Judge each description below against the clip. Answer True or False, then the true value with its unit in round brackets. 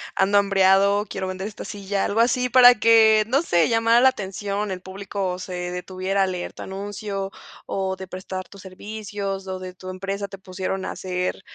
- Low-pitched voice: False (195 Hz)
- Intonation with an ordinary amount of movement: False (1.7 semitones)